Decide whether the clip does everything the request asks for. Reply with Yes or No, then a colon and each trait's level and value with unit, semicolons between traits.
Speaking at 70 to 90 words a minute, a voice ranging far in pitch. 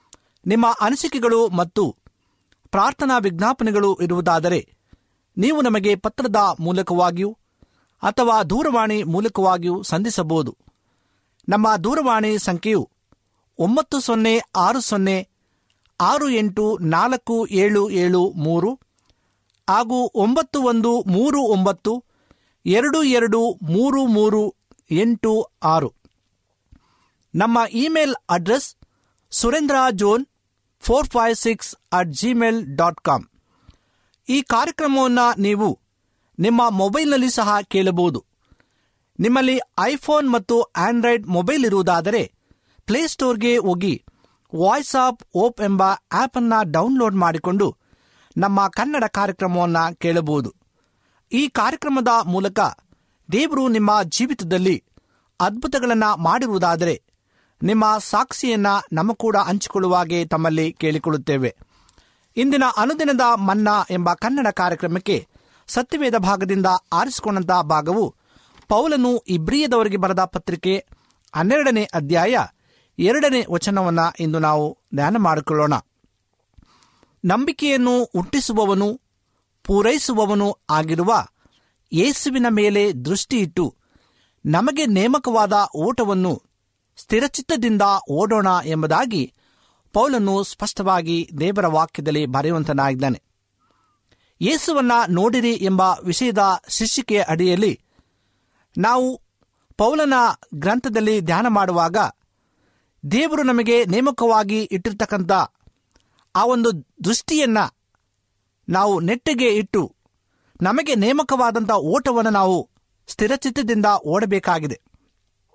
Yes: average, 85 wpm; wide, 5.7 semitones